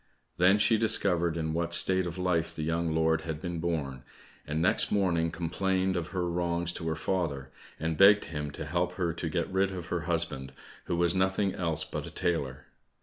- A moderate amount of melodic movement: No, narrow, 2.2 semitones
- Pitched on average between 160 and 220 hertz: No, very low, 85 Hz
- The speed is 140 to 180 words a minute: No, average, 200 wpm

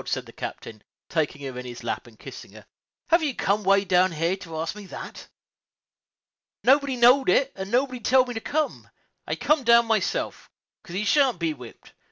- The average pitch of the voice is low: No, high, 205 Hz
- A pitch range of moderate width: No, wide, 7.6 semitones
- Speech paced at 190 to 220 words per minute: Yes, average, 200 wpm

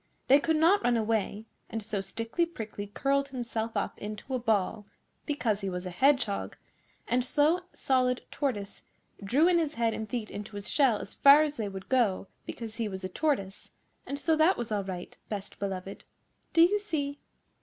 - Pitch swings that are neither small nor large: No, wide, 5.7 semitones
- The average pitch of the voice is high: Yes, high, 230 Hz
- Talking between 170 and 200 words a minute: Yes, average, 185 wpm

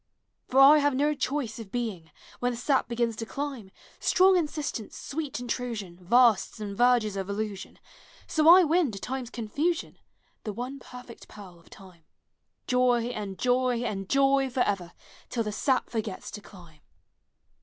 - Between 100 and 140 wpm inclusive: No, average, 165 wpm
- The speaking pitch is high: Yes, high, 245 Hz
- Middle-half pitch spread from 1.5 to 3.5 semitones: No, average, 4.7 semitones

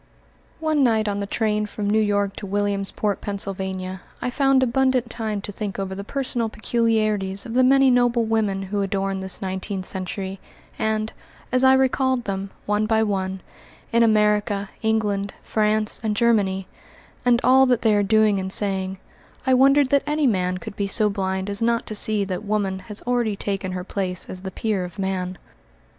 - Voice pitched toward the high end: Yes, high, 210 Hz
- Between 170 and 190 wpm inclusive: Yes, average, 180 wpm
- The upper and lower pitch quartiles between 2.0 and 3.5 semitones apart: Yes, average, 3.1 semitones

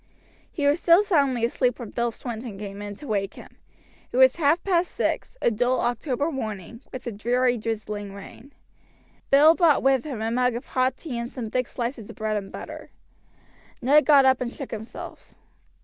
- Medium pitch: No, high, 245 Hz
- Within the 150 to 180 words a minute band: No, average, 190 wpm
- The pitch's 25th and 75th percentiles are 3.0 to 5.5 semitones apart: Yes, average, 3.9 semitones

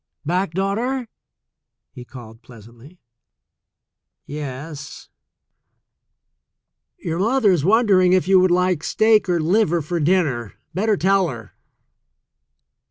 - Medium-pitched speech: Yes, medium, 180 Hz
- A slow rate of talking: Yes, slow, 100 wpm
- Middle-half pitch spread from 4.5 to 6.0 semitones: Yes, average, 5.1 semitones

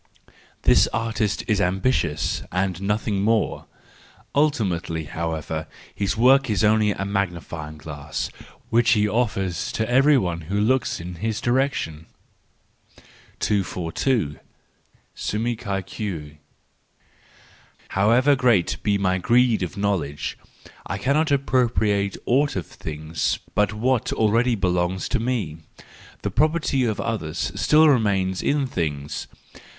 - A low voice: Yes, low, 100 Hz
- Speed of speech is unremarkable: No, slow, 115 wpm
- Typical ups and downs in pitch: No, wide, 5.7 semitones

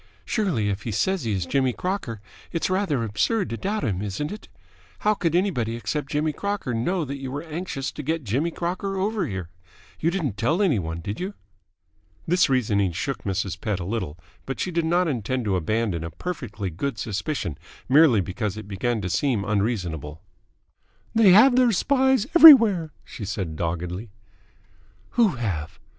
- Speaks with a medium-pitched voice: No, low, 130 Hz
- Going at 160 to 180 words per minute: Yes, average, 175 wpm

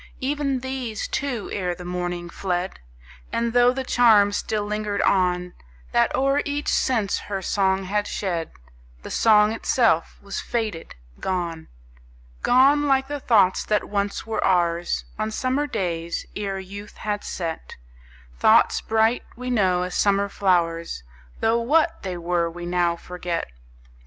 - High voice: Yes, high, 200 Hz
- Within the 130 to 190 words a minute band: Yes, average, 140 wpm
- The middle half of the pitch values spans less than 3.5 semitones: No, average, 5.0 semitones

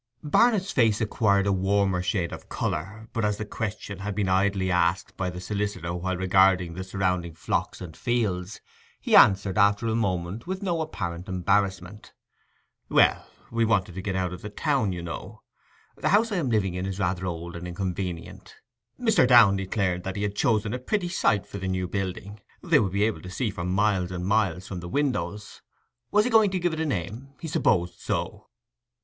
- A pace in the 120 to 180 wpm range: No, average, 195 wpm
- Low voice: Yes, low, 100 Hz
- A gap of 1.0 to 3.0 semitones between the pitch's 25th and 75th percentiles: No, average, 3.5 semitones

